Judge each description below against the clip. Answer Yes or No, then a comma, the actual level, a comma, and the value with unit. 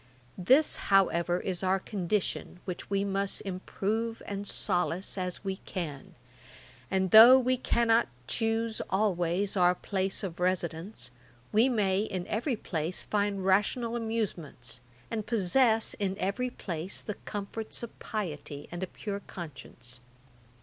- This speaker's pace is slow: Yes, slow, 130 wpm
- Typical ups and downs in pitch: Yes, average, 3.5 semitones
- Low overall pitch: No, high, 195 Hz